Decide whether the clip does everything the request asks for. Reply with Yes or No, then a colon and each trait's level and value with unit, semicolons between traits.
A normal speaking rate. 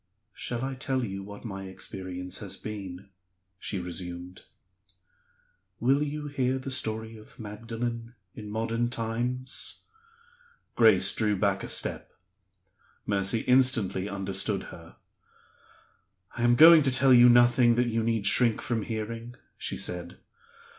No: slow, 130 wpm